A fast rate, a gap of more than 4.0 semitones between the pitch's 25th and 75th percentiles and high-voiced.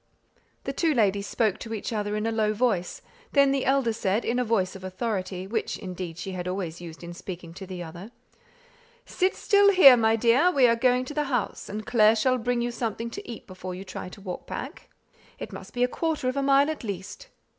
Yes: fast, 225 wpm; average, 5.1 semitones; high, 225 Hz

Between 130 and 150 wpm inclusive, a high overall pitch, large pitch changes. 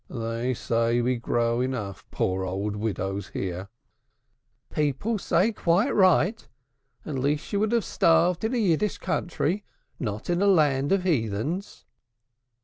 No: average, 140 wpm; medium, 140 Hz; wide, 8.5 semitones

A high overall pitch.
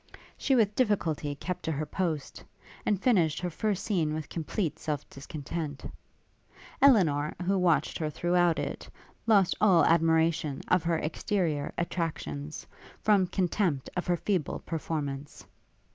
No: medium, 165 Hz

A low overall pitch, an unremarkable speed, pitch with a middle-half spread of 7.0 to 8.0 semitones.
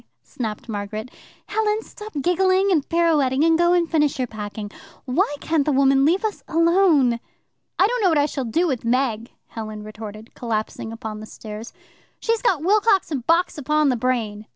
No: very high, 280 Hz; average, 175 wpm; wide, 7.4 semitones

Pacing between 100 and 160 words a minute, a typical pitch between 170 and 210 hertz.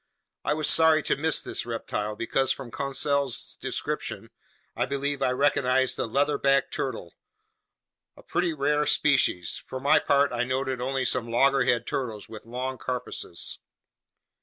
No: average, 140 wpm; low, 135 Hz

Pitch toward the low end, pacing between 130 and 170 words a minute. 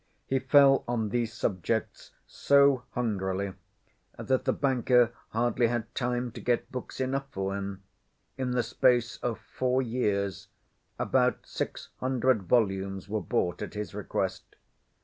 Yes: low, 120 Hz; slow, 135 wpm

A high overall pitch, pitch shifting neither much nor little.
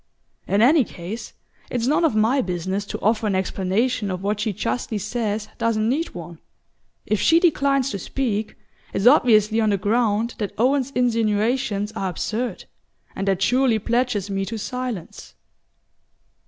Yes: high, 220 Hz; average, 3.5 semitones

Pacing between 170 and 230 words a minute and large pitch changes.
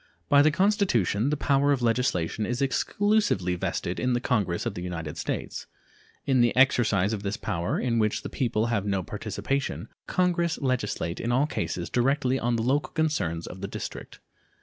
Yes: average, 175 wpm; wide, 6.1 semitones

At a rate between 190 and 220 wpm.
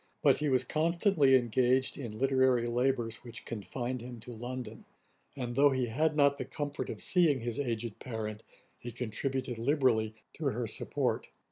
No: average, 160 wpm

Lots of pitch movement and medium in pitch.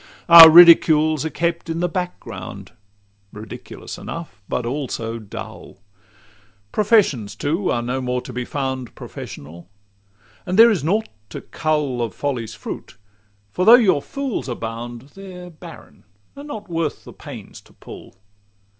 Yes: wide, 6.4 semitones; medium, 155 Hz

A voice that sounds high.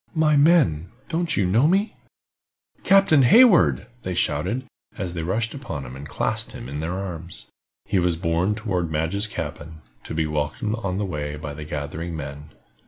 No: very low, 90 Hz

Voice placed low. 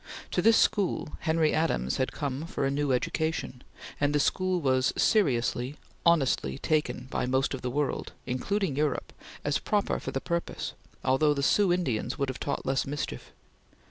No: medium, 145 Hz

